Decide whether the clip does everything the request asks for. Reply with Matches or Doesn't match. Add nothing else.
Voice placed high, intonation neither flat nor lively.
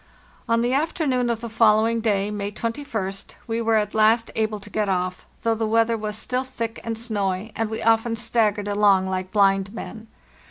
Doesn't match